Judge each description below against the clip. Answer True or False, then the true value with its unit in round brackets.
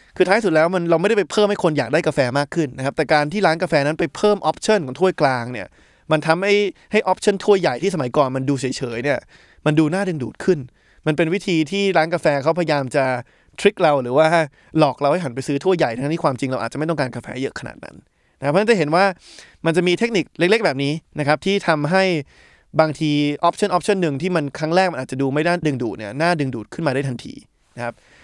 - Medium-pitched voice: True (160 Hz)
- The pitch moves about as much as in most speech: True (4.5 semitones)